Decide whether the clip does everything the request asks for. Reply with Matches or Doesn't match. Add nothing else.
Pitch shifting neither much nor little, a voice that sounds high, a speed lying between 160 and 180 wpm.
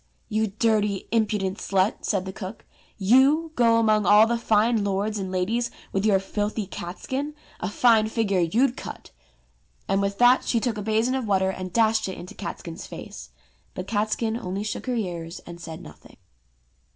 Matches